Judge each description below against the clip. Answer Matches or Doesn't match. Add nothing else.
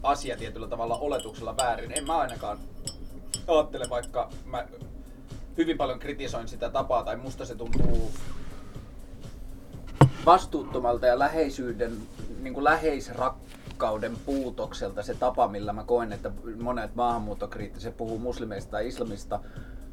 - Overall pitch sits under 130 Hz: Matches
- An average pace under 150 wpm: Matches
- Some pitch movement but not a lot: Matches